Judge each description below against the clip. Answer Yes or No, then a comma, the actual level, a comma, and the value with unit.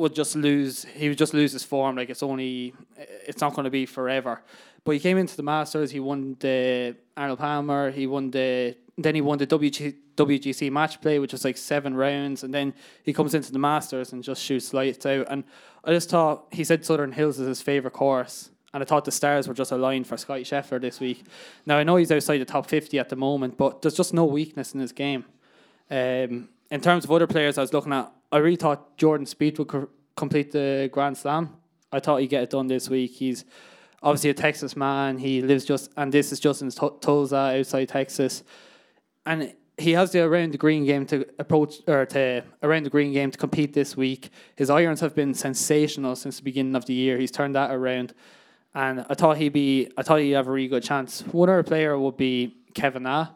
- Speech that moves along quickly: Yes, fast, 230 wpm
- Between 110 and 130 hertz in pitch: No, medium, 140 Hz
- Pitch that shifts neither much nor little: No, narrow, 2.1 semitones